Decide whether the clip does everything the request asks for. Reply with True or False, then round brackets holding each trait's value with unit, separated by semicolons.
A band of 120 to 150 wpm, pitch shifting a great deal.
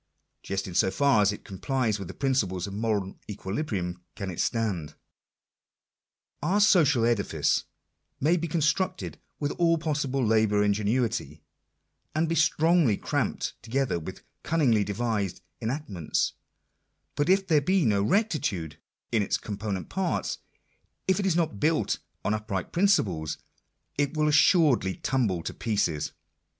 True (140 wpm; 7.7 semitones)